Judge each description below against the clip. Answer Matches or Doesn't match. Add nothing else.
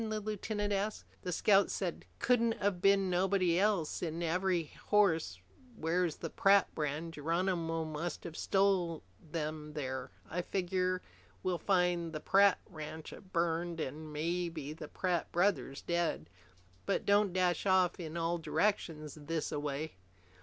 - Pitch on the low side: Doesn't match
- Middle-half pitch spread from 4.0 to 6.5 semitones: Doesn't match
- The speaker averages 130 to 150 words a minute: Matches